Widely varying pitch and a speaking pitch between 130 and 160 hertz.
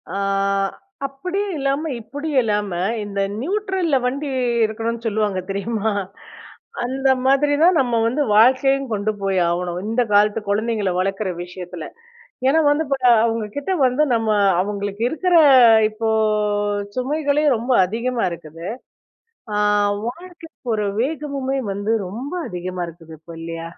No: wide, 5.7 semitones; high, 230 Hz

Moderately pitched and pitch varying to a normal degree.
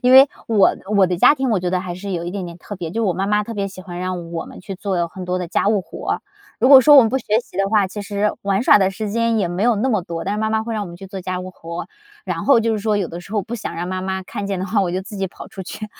No: high, 195 Hz; average, 3.0 semitones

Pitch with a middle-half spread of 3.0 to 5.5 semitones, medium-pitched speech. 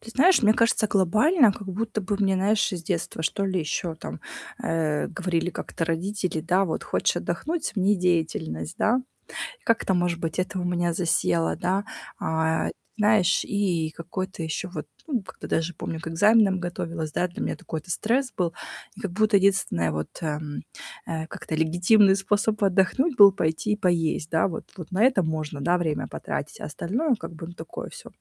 Yes: average, 4.0 semitones; medium, 180 Hz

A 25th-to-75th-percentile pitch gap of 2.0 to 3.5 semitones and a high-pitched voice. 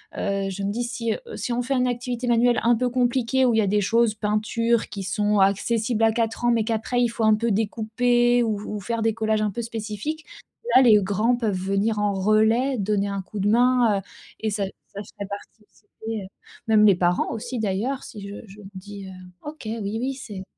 Yes: average, 2.8 semitones; high, 220 Hz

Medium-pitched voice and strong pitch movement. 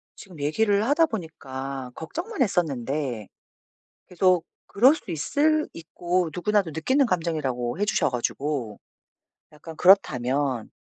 Yes: medium, 165 Hz; wide, 6.9 semitones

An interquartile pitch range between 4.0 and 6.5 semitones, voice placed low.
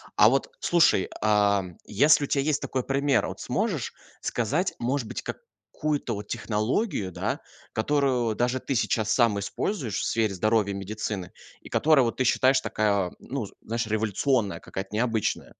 Yes: average, 4.6 semitones; low, 115 Hz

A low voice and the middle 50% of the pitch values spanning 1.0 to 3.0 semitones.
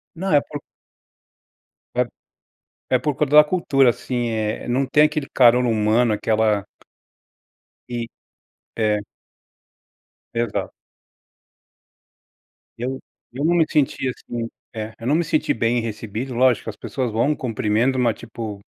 No: low, 120 Hz; average, 3.6 semitones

